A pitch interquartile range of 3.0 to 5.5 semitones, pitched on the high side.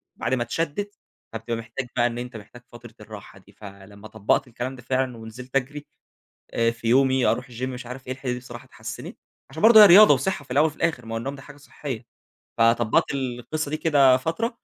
No: average, 3.5 semitones; low, 125 Hz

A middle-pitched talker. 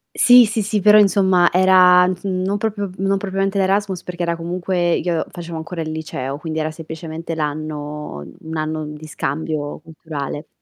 Yes: medium, 170 Hz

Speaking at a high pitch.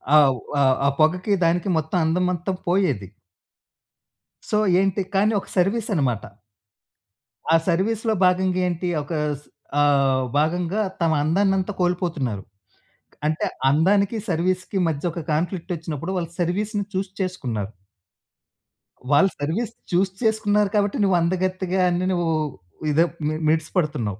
No: medium, 180 Hz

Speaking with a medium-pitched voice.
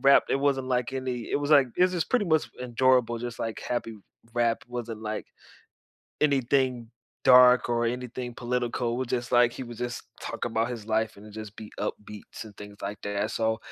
No: low, 120 Hz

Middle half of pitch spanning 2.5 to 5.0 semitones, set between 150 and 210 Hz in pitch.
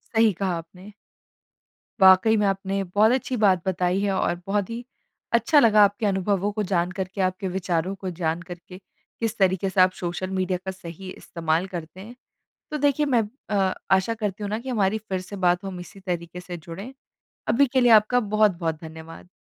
Yes: average, 3.0 semitones; high, 190 Hz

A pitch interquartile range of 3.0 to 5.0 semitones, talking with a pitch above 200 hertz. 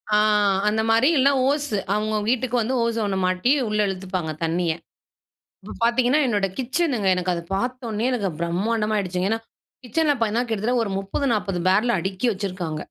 Yes: average, 4.3 semitones; high, 215 Hz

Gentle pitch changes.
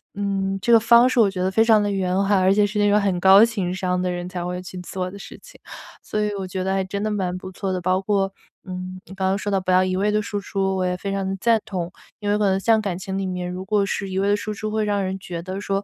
Yes: narrow, 1.8 semitones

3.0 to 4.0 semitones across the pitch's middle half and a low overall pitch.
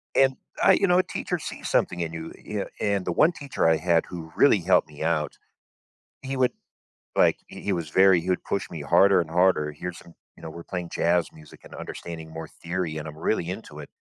Yes: average, 3.4 semitones; very low, 85 Hz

